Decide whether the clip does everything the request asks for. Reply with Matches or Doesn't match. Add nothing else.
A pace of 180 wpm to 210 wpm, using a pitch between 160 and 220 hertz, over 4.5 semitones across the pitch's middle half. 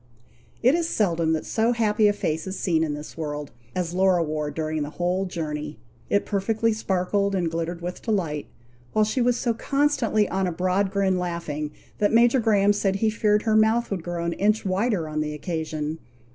Matches